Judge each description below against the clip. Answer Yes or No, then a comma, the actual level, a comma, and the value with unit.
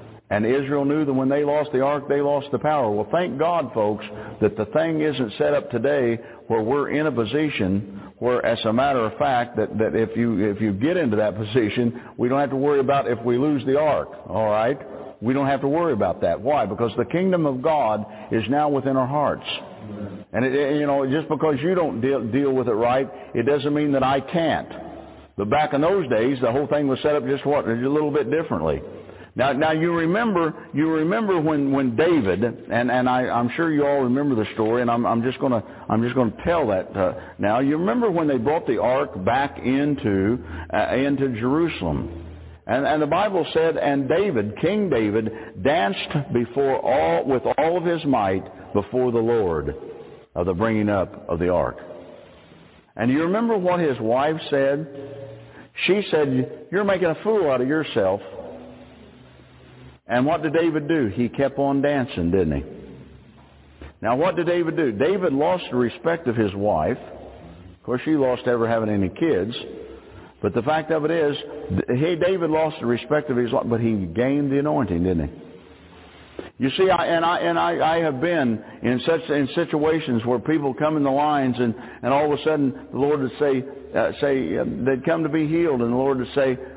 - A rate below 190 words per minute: No, fast, 205 wpm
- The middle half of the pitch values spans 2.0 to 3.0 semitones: No, average, 5.0 semitones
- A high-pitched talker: No, low, 135 Hz